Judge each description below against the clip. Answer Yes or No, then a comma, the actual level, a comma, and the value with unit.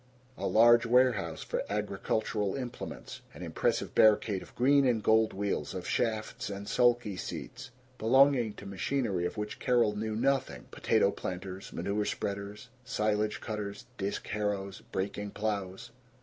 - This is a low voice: Yes, low, 105 Hz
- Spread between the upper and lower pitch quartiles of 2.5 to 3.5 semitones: Yes, average, 2.9 semitones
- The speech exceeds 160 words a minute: No, slow, 135 wpm